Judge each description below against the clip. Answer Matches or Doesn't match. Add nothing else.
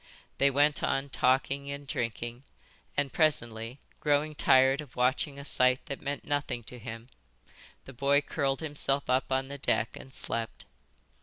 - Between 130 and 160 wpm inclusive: Matches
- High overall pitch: Doesn't match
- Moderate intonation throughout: Doesn't match